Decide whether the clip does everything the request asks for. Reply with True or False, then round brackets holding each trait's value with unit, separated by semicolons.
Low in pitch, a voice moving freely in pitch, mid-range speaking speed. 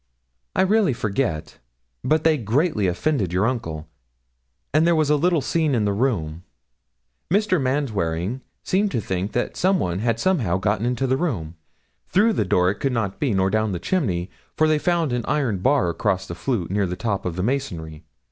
True (115 Hz; 8.2 semitones; 190 wpm)